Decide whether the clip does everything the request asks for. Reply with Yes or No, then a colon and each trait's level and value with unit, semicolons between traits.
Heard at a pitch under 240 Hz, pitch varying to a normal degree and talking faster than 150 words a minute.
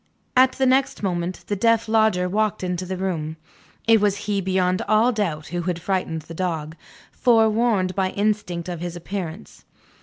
Yes: high, 190 Hz; average, 3.5 semitones; average, 170 wpm